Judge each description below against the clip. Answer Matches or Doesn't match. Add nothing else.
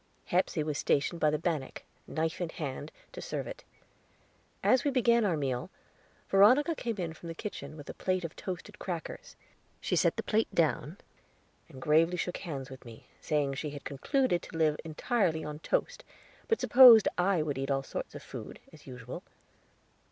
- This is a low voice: Doesn't match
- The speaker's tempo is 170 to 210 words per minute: Matches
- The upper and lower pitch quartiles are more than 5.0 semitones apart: Matches